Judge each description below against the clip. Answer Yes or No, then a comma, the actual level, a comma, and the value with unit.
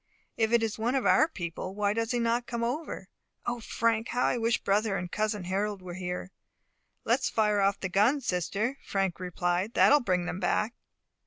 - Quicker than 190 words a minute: Yes, average, 200 wpm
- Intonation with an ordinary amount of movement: Yes, average, 3.9 semitones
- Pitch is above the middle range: Yes, high, 210 Hz